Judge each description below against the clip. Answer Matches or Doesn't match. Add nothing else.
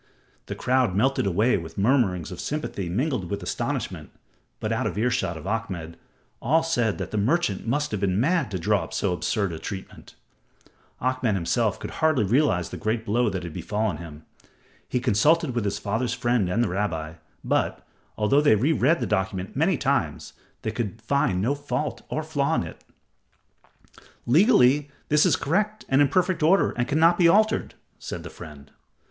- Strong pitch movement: Matches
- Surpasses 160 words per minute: Matches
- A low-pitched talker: Matches